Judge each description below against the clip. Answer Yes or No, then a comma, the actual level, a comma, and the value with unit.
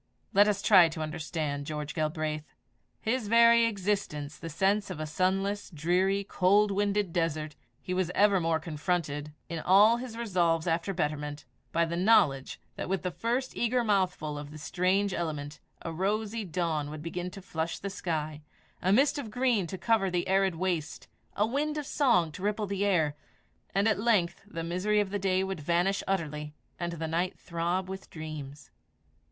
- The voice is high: No, medium, 180 Hz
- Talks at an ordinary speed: Yes, average, 175 wpm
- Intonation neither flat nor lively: Yes, average, 4.3 semitones